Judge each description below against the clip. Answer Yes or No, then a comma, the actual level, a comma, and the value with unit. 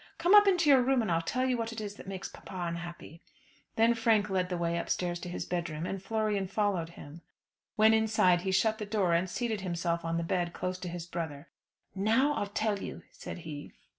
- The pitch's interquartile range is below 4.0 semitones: No, average, 4.3 semitones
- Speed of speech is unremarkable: No, fast, 220 wpm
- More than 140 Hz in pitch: Yes, high, 190 Hz